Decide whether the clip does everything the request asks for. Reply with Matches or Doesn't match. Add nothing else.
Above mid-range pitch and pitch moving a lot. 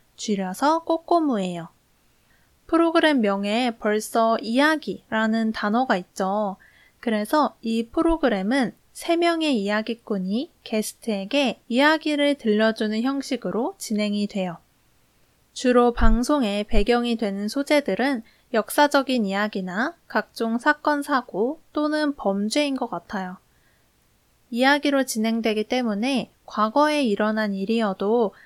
Doesn't match